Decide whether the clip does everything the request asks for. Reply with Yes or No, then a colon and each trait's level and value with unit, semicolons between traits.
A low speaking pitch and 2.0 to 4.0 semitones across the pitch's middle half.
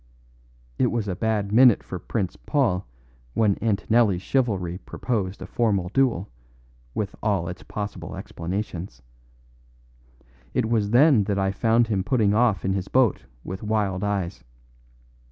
Yes: low, 105 Hz; average, 3.4 semitones